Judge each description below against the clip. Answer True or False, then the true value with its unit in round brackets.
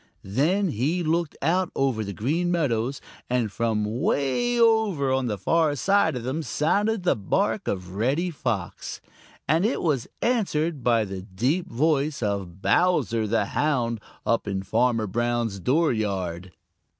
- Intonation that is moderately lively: False (7.4 semitones)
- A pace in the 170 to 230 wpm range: False (145 wpm)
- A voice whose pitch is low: True (130 Hz)